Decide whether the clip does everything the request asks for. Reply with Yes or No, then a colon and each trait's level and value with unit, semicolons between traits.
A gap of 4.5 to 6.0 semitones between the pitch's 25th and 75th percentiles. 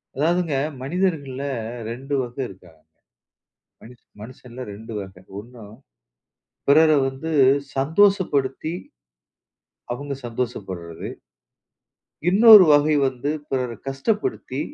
Yes: average, 4.9 semitones